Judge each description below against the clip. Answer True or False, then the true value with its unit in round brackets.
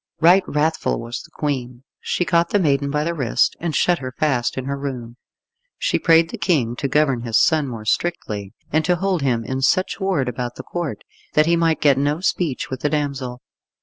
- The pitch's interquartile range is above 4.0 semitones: True (4.8 semitones)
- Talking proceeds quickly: True (210 wpm)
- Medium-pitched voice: True (145 Hz)